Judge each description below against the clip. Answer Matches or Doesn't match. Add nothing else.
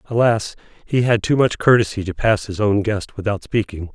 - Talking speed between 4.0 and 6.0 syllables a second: Matches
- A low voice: Matches